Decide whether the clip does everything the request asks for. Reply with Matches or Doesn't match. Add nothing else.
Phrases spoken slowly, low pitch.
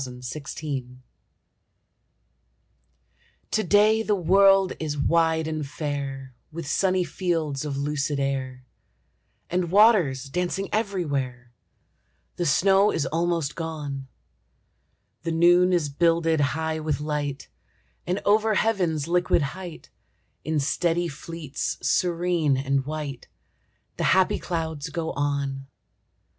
Doesn't match